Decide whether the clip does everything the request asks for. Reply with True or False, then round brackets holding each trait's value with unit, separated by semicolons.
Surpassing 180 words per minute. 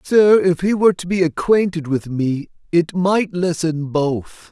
False (175 wpm)